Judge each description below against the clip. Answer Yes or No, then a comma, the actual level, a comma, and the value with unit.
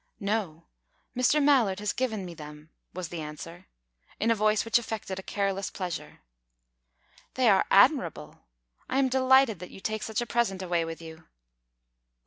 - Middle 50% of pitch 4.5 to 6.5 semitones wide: Yes, average, 5.2 semitones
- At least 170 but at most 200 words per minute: No, average, 160 wpm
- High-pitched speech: Yes, high, 195 Hz